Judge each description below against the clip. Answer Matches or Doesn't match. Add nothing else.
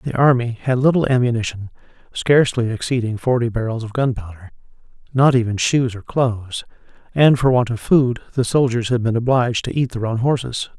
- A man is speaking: Matches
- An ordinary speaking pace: Matches